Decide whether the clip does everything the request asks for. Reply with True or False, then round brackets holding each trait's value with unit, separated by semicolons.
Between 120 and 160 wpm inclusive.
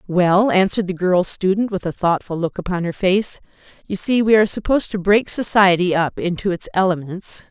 False (190 wpm)